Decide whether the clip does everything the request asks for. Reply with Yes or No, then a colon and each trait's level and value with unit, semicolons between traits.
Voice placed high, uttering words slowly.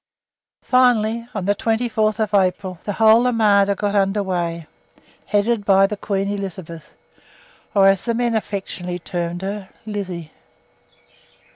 Yes: high, 200 Hz; slow, 125 wpm